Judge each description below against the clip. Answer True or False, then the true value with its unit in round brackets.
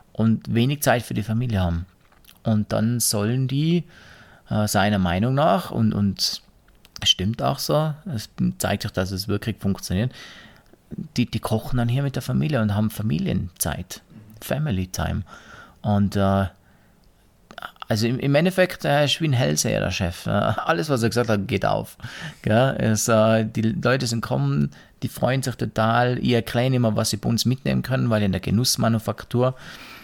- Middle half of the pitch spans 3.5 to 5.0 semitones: True (3.8 semitones)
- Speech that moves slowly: False (165 wpm)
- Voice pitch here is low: True (110 Hz)